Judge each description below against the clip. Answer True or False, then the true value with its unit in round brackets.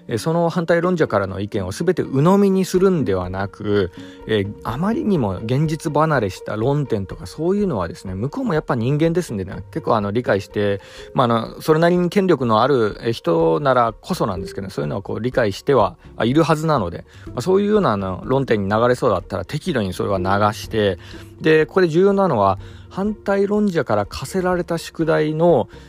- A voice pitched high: False (125 Hz)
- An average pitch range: False (9.0 semitones)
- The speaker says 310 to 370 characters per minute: False (395 characters per minute)